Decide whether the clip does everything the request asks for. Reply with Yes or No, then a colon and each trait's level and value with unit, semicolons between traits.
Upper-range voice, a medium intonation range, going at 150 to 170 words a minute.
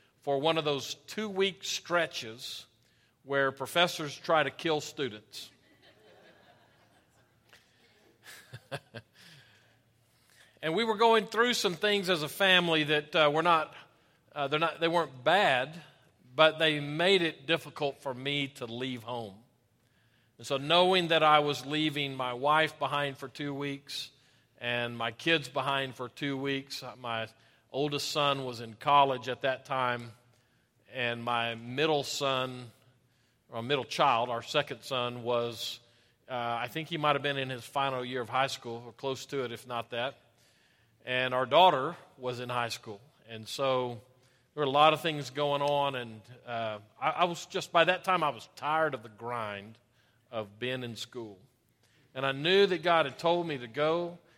No: low, 135 Hz; average, 4.1 semitones; average, 165 wpm